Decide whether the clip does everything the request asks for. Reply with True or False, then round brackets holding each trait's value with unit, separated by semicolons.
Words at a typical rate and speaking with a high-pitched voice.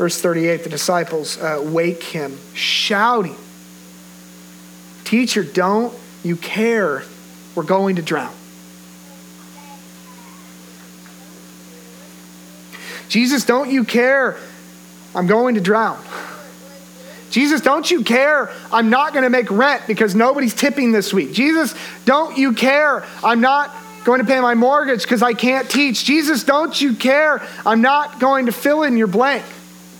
False (130 wpm; 210 Hz)